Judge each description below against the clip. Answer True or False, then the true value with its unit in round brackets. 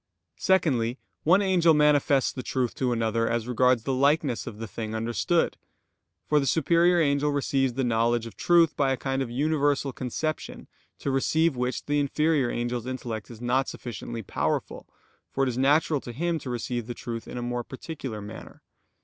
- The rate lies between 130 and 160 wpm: False (175 wpm)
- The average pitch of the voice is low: True (130 Hz)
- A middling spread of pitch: True (3.8 semitones)